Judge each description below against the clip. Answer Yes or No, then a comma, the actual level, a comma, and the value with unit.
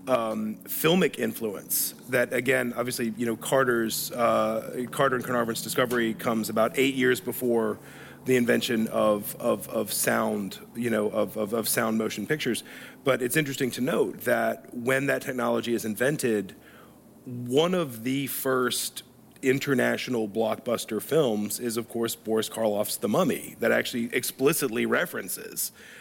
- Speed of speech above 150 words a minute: No, average, 145 wpm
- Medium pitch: No, low, 120 Hz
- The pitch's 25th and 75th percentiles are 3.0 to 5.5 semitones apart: No, narrow, 2.6 semitones